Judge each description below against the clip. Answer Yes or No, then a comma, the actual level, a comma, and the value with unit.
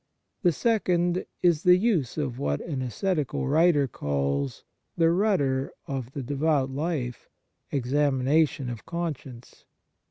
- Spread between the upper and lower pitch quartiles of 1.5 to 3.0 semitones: No, average, 5.0 semitones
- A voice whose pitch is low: No, medium, 145 Hz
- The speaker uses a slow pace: Yes, slow, 125 wpm